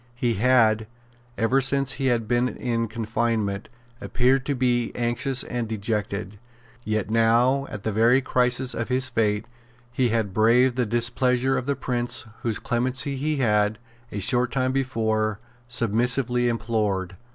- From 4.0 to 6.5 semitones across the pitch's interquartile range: No, narrow, 2.5 semitones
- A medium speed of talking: Yes, average, 145 wpm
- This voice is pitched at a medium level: No, low, 120 Hz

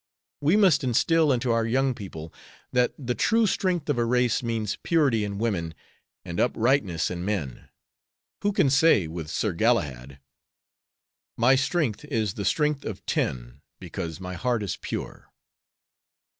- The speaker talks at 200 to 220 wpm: No, average, 145 wpm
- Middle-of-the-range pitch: No, low, 115 Hz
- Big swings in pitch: Yes, wide, 6.7 semitones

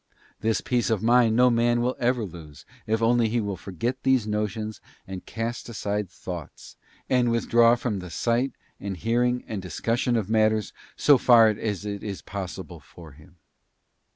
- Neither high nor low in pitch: No, low, 110 Hz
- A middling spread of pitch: Yes, average, 3.3 semitones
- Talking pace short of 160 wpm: No, average, 170 wpm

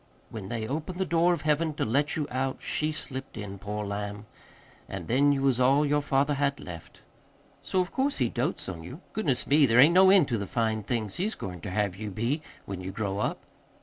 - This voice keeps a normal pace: No, fast, 225 wpm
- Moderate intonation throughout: No, wide, 6.2 semitones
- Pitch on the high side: No, low, 130 Hz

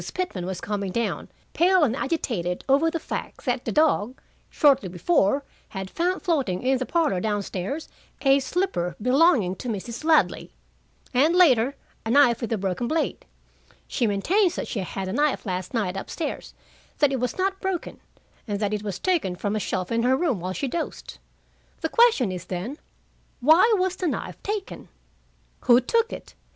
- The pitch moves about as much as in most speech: No, wide, 8.5 semitones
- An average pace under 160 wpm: No, average, 180 wpm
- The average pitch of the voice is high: Yes, very high, 250 Hz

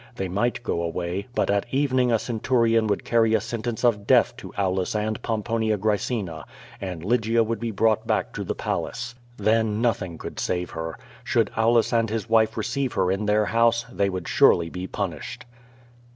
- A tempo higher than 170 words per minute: Yes, average, 180 wpm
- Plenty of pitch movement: No, average, 3.1 semitones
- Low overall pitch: Yes, low, 110 Hz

